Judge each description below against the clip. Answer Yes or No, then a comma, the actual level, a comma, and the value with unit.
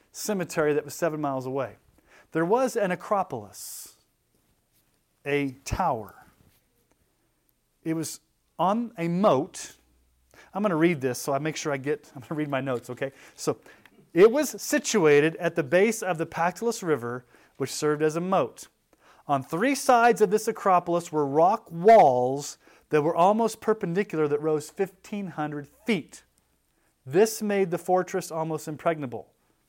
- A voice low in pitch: No, medium, 165 Hz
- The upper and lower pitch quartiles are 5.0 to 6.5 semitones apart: Yes, average, 5.3 semitones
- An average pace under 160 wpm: Yes, average, 150 wpm